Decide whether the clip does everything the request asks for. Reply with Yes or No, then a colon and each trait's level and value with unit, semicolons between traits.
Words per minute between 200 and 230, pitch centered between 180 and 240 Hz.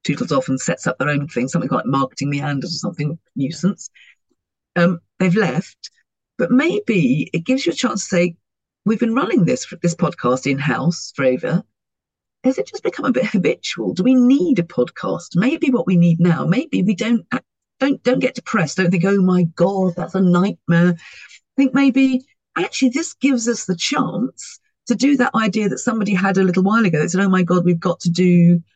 Yes: fast, 205 wpm; high, 190 Hz